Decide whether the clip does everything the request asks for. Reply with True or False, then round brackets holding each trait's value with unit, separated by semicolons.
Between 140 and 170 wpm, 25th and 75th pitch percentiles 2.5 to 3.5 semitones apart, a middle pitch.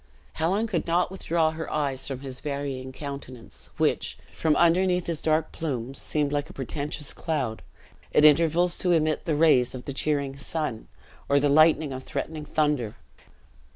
True (160 wpm; 2.9 semitones; 150 Hz)